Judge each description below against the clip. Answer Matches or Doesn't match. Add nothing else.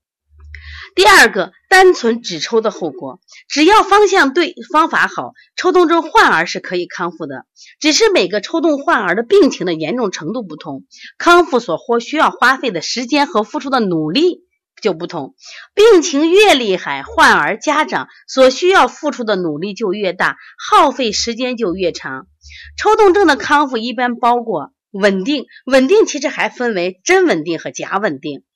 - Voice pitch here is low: Doesn't match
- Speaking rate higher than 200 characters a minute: Matches